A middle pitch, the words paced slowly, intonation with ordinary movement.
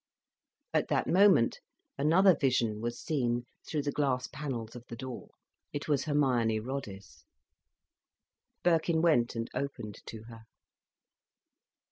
No: low, 130 Hz; slow, 120 wpm; average, 4.4 semitones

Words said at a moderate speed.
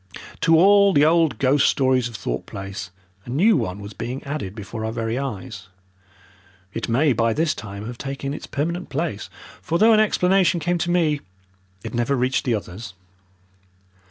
Yes: average, 175 wpm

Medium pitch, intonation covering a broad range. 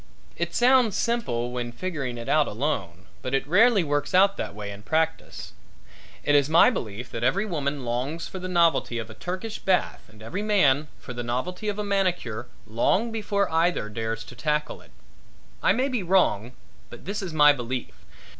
Yes: medium, 150 Hz; wide, 8.1 semitones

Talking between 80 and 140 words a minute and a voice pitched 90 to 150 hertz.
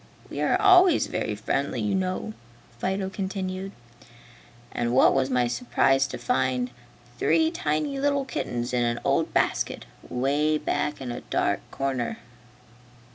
Yes: slow, 135 wpm; medium, 140 Hz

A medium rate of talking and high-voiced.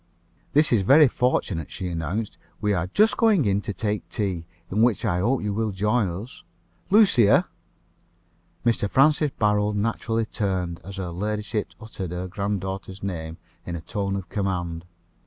No: average, 155 wpm; low, 100 Hz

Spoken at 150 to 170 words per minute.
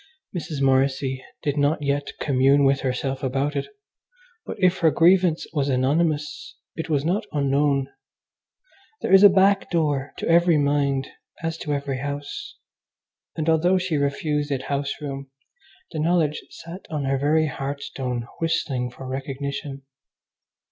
No: average, 140 wpm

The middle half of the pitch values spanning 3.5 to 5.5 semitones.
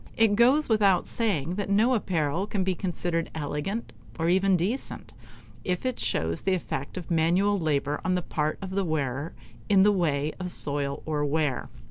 Yes: average, 4.9 semitones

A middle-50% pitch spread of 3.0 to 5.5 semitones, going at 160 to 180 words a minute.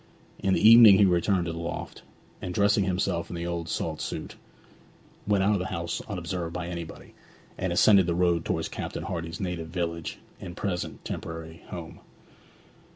No: narrow, 2.4 semitones; average, 170 wpm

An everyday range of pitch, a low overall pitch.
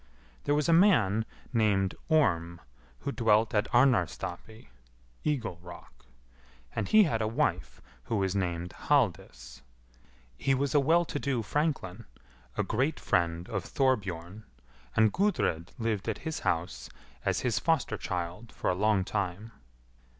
No: wide, 7.1 semitones; low, 110 Hz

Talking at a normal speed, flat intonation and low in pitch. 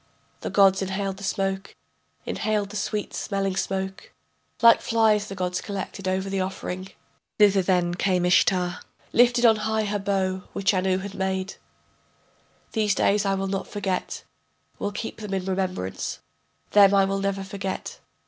No: average, 155 wpm; narrow, 1.3 semitones; high, 195 Hz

